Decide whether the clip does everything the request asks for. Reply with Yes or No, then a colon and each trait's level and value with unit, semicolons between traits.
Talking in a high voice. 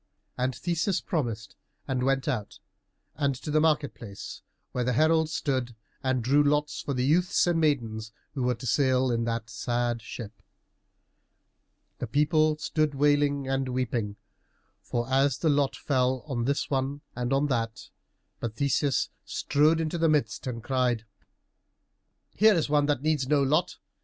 No: low, 135 Hz